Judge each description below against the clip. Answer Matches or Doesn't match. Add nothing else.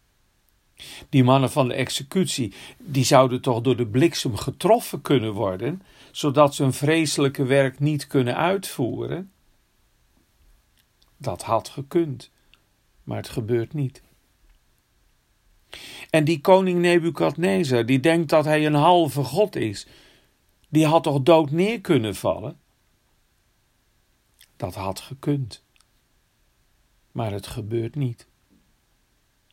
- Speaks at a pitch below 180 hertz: Matches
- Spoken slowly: Matches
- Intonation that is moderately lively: Matches